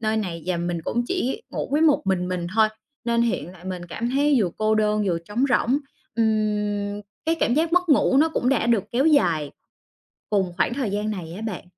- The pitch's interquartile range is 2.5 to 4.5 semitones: No, average, 5.2 semitones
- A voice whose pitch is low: No, high, 215 Hz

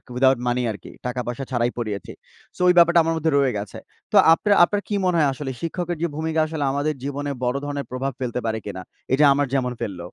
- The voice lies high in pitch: No, medium, 140 Hz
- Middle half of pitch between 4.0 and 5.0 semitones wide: Yes, average, 4.5 semitones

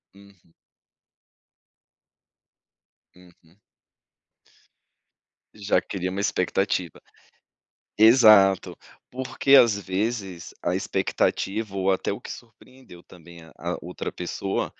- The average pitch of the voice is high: No, very low, 95 Hz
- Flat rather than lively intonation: No, average, 3.2 semitones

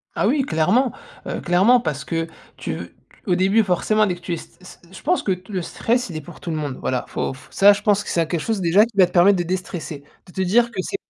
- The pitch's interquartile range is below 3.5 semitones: No, average, 4.1 semitones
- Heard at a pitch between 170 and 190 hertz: Yes, medium, 185 Hz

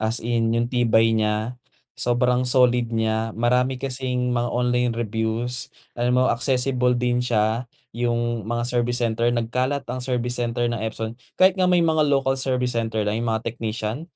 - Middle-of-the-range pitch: No, low, 120 Hz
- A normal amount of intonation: No, narrow, 1.7 semitones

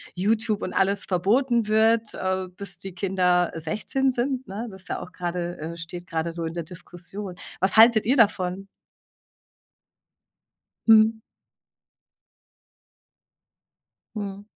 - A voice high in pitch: Yes, high, 195 Hz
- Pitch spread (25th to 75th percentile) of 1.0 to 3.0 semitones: No, average, 3.6 semitones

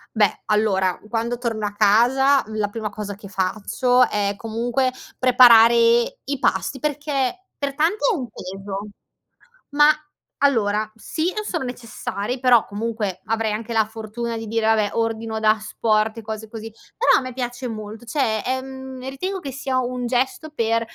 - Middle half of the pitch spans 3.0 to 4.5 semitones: Yes, average, 3.3 semitones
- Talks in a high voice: Yes, high, 230 Hz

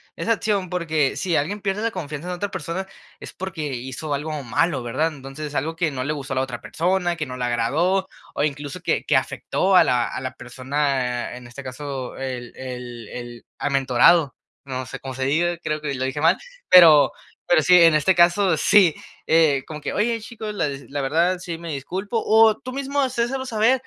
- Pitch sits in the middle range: Yes, medium, 155 Hz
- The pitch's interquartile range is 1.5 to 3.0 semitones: No, wide, 5.6 semitones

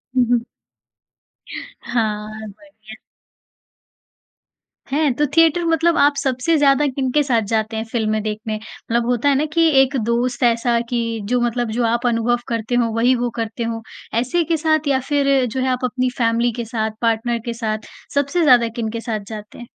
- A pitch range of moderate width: Yes, average, 3.2 semitones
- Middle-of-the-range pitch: No, high, 240 Hz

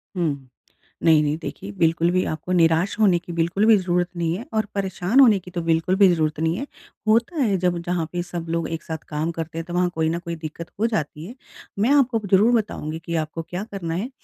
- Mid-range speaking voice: Yes, medium, 170 Hz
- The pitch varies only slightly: No, average, 3.2 semitones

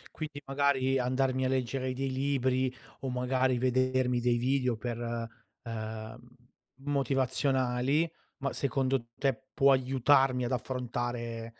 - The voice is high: No, low, 130 Hz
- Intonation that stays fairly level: Yes, narrow, 1.5 semitones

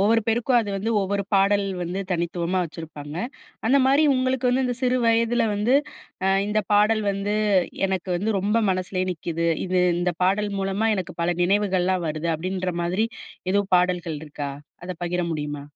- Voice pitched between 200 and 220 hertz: No, high, 190 Hz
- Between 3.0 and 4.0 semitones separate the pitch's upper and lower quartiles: Yes, average, 3.5 semitones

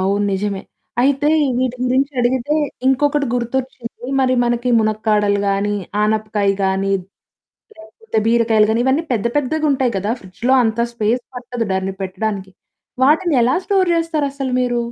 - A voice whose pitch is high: Yes, high, 240 Hz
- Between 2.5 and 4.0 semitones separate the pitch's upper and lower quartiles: No, average, 4.5 semitones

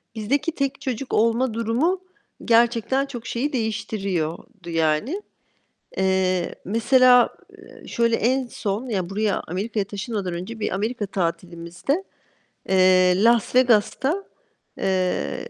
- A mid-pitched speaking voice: No, high, 220 Hz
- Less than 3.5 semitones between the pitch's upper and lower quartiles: No, average, 4.8 semitones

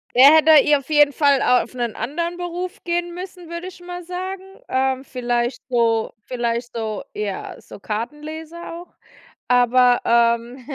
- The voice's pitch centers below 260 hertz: No, very high, 275 Hz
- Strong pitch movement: Yes, wide, 6.1 semitones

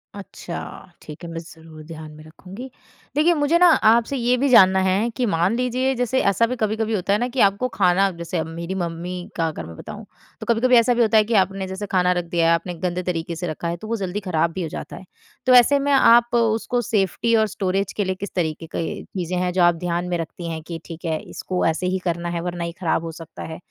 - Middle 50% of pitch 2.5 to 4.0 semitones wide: No, average, 5.1 semitones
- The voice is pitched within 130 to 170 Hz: No, medium, 185 Hz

